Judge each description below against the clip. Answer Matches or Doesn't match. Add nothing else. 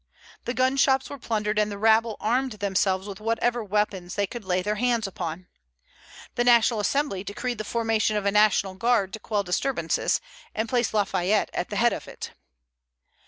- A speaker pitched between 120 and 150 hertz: Doesn't match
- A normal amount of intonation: Matches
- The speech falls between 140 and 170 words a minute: Doesn't match